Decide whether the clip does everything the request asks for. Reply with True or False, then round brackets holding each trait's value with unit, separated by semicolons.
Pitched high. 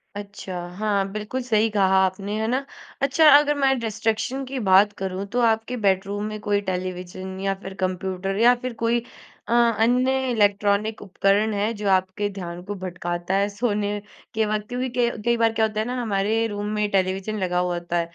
True (205 Hz)